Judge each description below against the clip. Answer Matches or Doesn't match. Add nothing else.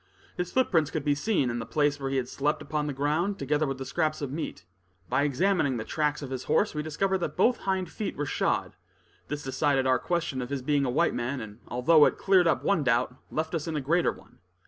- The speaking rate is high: Matches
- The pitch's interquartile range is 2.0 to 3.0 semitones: Doesn't match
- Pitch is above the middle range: Doesn't match